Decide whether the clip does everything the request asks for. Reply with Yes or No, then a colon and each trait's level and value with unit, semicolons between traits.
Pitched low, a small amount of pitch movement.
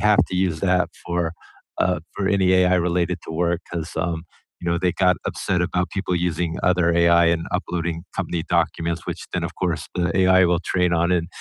Yes: very low, 90 Hz; narrow, 1.3 semitones